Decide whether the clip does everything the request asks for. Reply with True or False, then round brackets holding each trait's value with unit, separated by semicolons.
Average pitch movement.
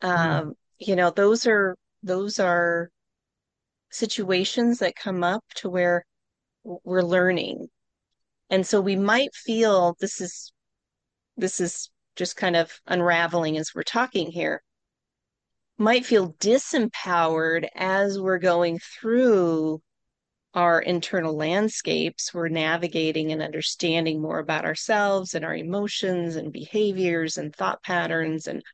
True (3.3 semitones)